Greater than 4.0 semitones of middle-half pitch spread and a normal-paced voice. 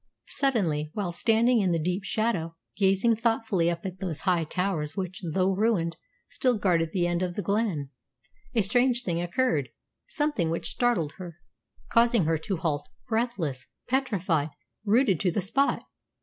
Yes: average, 5.3 semitones; average, 155 wpm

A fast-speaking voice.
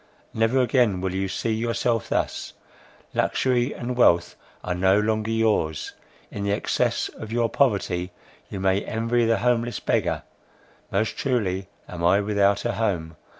No: average, 150 wpm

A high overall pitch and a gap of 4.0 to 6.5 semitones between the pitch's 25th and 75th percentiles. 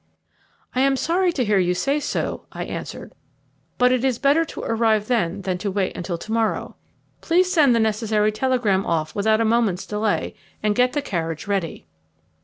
Yes: high, 220 Hz; average, 4.5 semitones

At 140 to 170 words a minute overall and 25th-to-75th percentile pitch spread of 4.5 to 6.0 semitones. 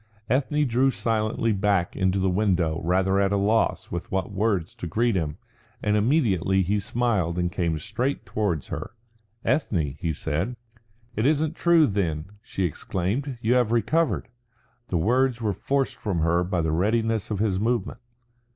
Yes: average, 160 wpm; average, 4.9 semitones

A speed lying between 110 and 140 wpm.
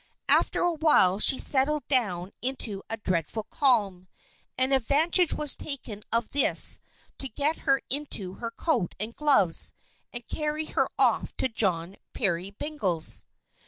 Yes: slow, 135 wpm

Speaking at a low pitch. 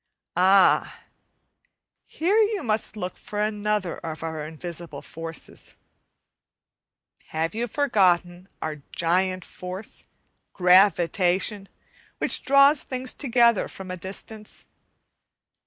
No: high, 190 Hz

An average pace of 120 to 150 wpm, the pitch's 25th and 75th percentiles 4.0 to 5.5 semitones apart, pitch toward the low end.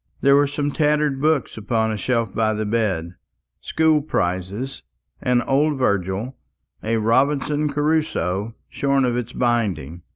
Yes: slow, 135 wpm; average, 5.2 semitones; low, 125 Hz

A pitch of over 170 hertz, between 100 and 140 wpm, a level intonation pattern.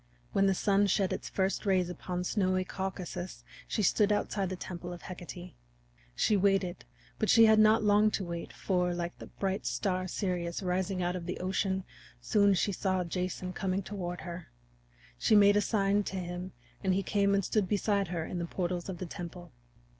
No: medium, 185 Hz; average, 185 wpm; narrow, 2.0 semitones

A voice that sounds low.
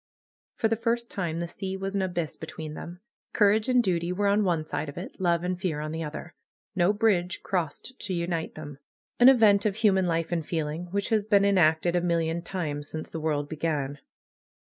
No: medium, 175 Hz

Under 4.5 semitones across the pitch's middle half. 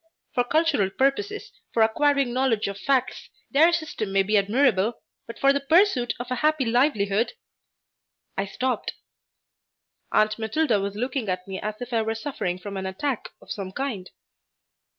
No: wide, 5.5 semitones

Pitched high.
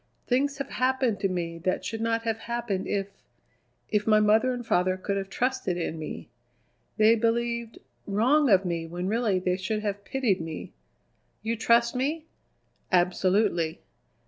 Yes: high, 215 Hz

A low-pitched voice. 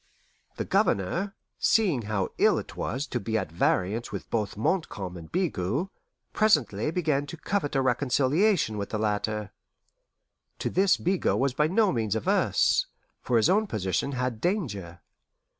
Yes: low, 125 Hz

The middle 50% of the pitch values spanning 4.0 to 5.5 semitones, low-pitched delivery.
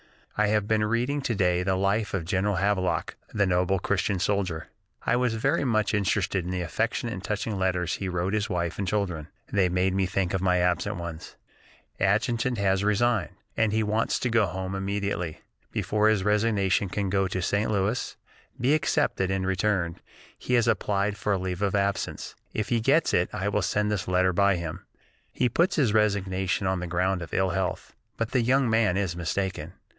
No: narrow, 2.6 semitones; low, 100 Hz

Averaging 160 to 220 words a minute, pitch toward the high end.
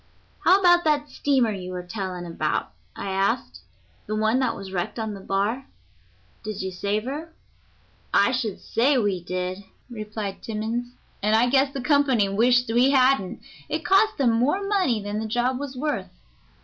Yes: average, 170 wpm; high, 230 Hz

